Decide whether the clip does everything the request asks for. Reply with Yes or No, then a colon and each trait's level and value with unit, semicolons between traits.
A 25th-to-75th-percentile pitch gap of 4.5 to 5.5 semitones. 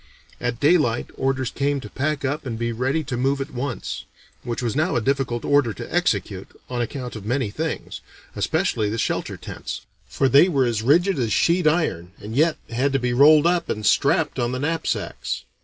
No: average, 3.9 semitones